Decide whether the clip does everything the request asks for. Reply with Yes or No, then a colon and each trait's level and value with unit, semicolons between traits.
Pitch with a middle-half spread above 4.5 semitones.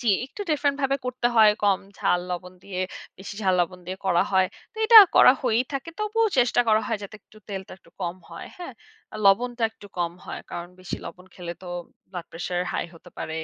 Yes: wide, 5.6 semitones